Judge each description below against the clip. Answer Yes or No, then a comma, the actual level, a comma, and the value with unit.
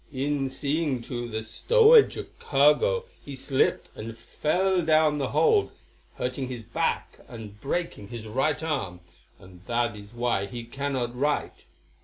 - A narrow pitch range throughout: No, average, 4.6 semitones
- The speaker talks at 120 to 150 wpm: Yes, average, 145 wpm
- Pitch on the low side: Yes, low, 130 Hz